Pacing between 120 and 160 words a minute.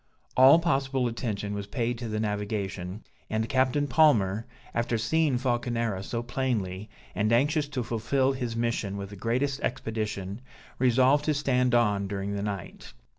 Yes: average, 150 wpm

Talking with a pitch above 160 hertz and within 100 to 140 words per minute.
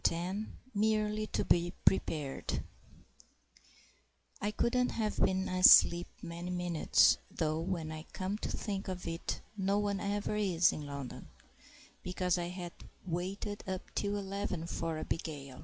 Yes: medium, 185 Hz; slow, 135 wpm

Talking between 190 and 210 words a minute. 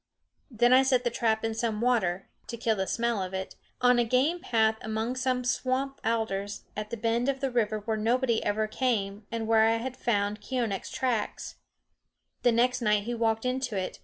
Yes: average, 195 wpm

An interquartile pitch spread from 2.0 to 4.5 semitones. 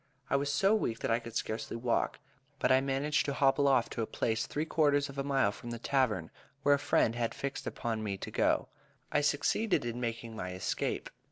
Yes: average, 3.8 semitones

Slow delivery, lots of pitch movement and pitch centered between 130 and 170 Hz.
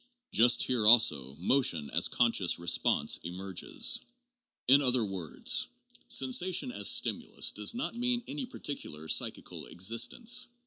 No: slow, 125 wpm; wide, 8.4 semitones; low, 120 Hz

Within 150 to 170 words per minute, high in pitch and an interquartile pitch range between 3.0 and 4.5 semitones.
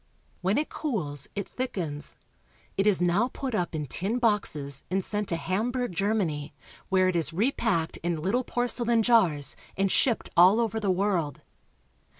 No: average, 155 wpm; high, 195 Hz; average, 5.2 semitones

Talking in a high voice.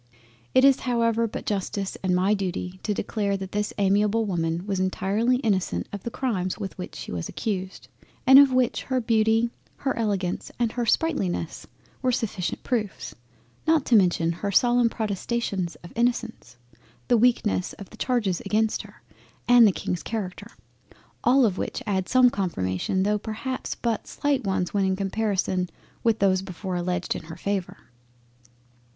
Yes: high, 205 Hz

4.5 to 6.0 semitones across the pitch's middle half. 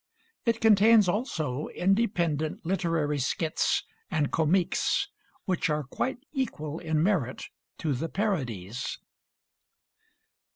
Yes: average, 5.2 semitones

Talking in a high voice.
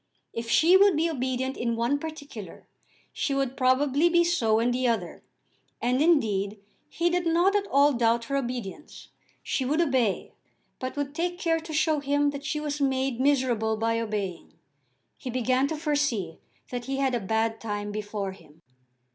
Yes: very high, 260 Hz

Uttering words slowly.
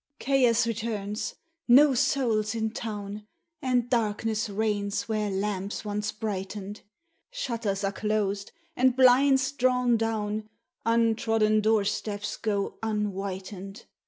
Yes: slow, 105 wpm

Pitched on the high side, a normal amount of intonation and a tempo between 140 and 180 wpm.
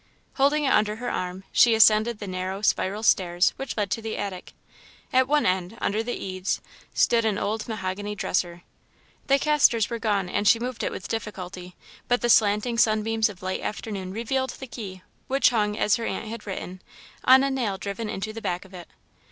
No: high, 215 Hz; average, 3.5 semitones; average, 195 wpm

